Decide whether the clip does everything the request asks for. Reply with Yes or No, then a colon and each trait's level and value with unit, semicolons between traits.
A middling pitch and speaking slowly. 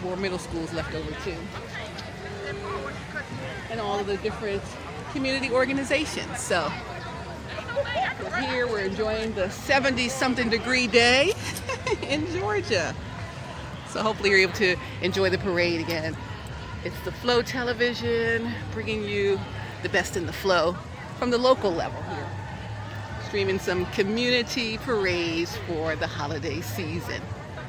Yes: medium, 180 Hz; slow, 125 wpm